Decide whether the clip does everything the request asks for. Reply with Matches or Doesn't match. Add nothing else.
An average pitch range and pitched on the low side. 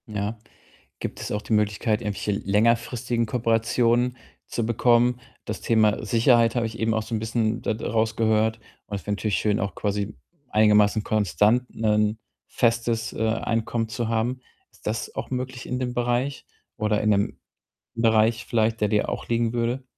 Doesn't match